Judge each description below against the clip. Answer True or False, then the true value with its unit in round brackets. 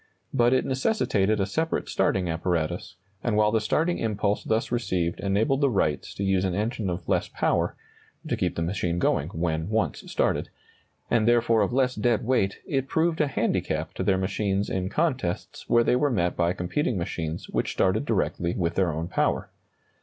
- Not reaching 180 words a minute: False (185 wpm)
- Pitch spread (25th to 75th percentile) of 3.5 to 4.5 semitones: False (5.2 semitones)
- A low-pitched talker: True (105 Hz)